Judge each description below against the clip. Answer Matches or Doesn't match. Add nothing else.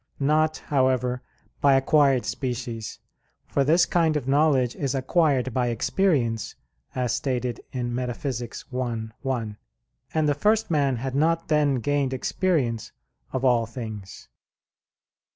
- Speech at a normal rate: Doesn't match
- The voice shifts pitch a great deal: Doesn't match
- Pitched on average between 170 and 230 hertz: Doesn't match